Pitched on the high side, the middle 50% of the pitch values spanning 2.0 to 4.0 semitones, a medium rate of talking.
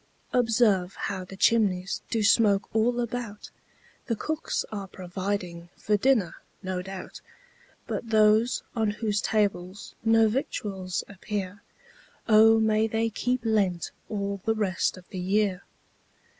No: high, 210 Hz; average, 2.8 semitones; slow, 130 wpm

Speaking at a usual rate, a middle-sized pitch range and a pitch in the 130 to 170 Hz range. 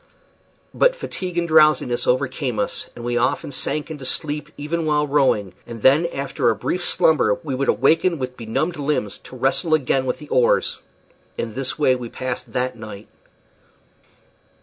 Yes: average, 165 wpm; average, 3.7 semitones; low, 135 Hz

